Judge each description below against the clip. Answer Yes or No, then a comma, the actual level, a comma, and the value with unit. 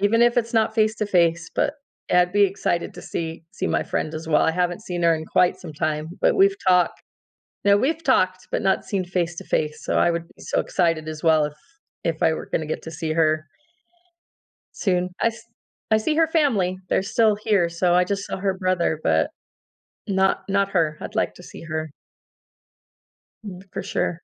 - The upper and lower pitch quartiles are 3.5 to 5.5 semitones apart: Yes, average, 3.9 semitones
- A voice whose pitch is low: No, medium, 180 Hz